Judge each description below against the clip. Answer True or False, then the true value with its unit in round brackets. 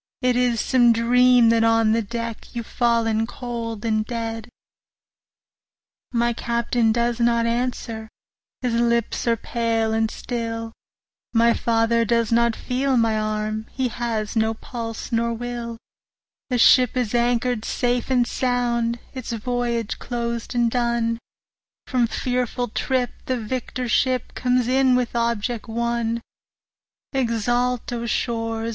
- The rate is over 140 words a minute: False (135 wpm)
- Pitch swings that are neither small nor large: False (1.3 semitones)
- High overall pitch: True (235 Hz)